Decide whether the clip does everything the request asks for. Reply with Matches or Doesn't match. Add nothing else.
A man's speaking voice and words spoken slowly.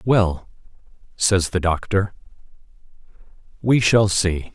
Matches